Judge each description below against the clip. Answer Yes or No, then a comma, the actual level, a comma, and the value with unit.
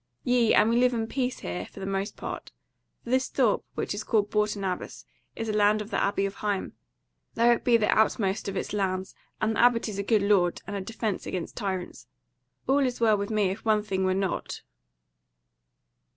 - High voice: Yes, high, 210 Hz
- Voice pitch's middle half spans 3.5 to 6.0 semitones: No, average, 2.7 semitones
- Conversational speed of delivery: No, fast, 210 wpm